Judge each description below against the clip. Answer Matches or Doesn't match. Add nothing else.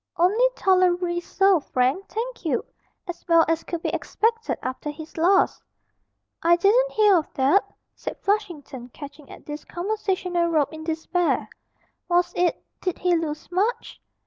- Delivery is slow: Doesn't match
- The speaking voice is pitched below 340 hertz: Doesn't match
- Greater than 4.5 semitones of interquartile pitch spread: Doesn't match